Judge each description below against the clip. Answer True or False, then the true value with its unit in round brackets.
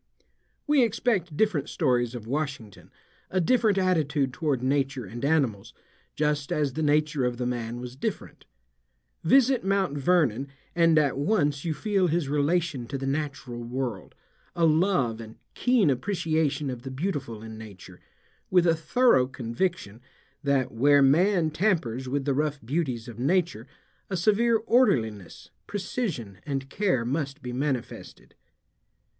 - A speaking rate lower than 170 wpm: True (140 wpm)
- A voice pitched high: False (145 Hz)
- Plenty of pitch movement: True (5.7 semitones)